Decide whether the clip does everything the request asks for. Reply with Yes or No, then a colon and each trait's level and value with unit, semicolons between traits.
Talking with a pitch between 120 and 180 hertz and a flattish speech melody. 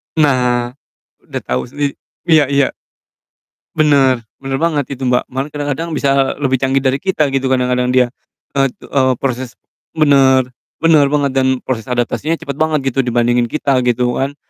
Yes: low, 135 Hz; narrow, 2.3 semitones